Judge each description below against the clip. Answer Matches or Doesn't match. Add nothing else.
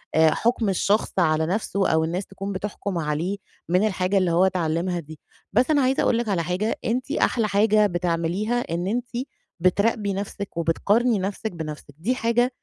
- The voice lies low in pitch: Doesn't match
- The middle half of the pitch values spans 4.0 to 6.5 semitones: Matches